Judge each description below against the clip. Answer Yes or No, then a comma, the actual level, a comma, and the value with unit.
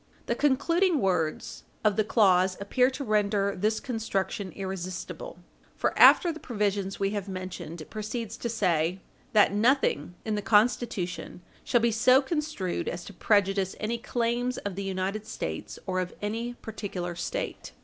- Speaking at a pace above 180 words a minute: No, average, 155 wpm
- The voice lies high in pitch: Yes, high, 205 Hz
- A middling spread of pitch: Yes, average, 3.9 semitones